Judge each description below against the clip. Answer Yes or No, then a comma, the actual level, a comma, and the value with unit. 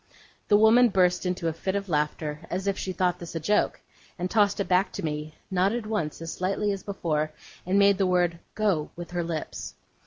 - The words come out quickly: Yes, fast, 210 wpm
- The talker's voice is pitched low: No, medium, 185 Hz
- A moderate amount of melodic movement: Yes, average, 3.2 semitones